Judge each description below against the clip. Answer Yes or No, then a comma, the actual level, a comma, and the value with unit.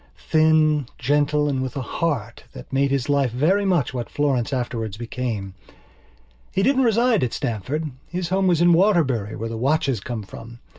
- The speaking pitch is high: No, medium, 140 Hz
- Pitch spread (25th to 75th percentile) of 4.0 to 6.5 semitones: Yes, wide, 5.6 semitones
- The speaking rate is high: No, average, 170 wpm